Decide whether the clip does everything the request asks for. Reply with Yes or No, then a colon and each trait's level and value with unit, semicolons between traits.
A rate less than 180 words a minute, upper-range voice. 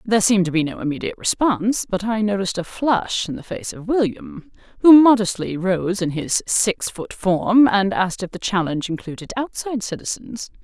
No: average, 185 wpm; high, 205 Hz